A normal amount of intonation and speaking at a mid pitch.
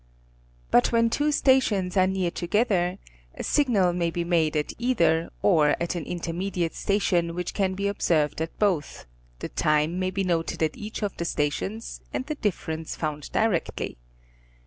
Yes: average, 3.8 semitones; medium, 180 Hz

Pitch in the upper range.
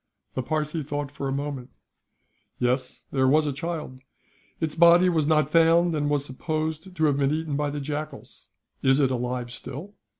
No: medium, 145 Hz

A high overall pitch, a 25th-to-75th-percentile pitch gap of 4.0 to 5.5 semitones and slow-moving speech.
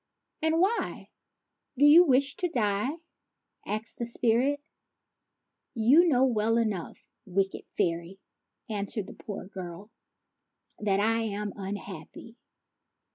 Yes: high, 220 Hz; average, 4.6 semitones; slow, 125 wpm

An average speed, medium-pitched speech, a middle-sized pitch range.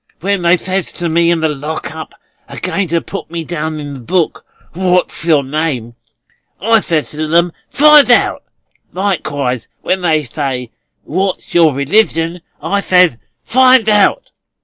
Yes: average, 155 wpm; medium, 170 Hz; average, 3.8 semitones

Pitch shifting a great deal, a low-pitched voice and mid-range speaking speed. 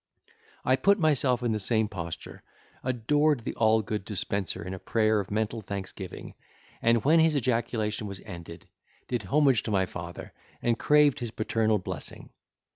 No: average, 4.0 semitones; low, 110 Hz; average, 160 wpm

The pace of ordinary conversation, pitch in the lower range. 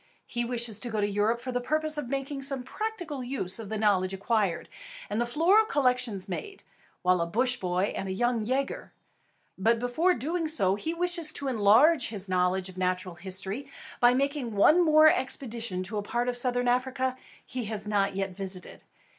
No: average, 190 wpm; high, 240 Hz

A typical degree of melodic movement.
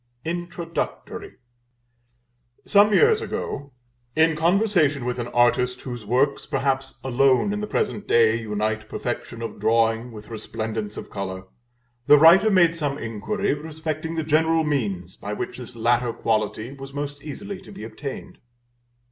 No: wide, 6.0 semitones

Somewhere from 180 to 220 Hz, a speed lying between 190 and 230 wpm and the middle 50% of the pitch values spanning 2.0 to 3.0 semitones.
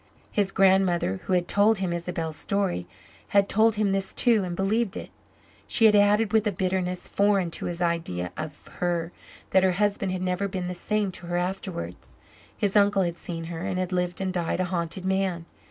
Yes: medium, 185 Hz; average, 200 wpm; narrow, 2.4 semitones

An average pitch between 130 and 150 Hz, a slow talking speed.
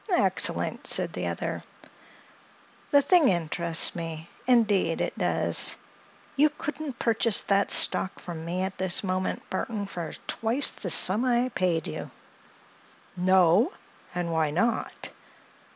No: high, 190 Hz; slow, 120 wpm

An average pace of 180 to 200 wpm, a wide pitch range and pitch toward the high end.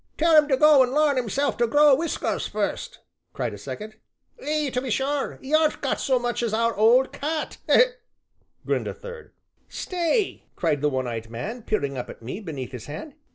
Yes: average, 195 wpm; wide, 6.4 semitones; very high, 255 Hz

